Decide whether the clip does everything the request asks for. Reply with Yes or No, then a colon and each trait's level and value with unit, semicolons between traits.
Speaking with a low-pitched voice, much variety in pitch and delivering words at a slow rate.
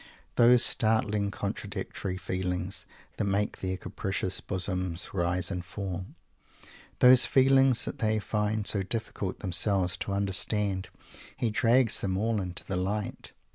No: low, 100 Hz; average, 2.8 semitones; slow, 130 wpm